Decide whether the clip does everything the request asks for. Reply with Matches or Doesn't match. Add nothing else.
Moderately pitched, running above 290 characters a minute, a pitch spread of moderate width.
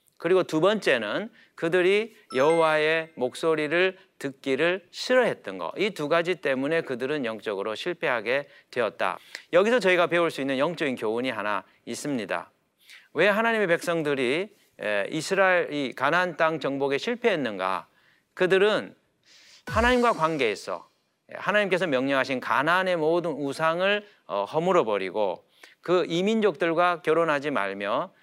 Matches